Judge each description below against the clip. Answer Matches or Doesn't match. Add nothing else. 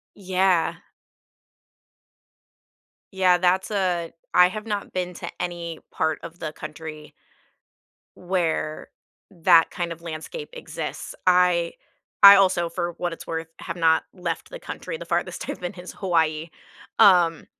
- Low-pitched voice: Doesn't match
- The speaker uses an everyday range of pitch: Doesn't match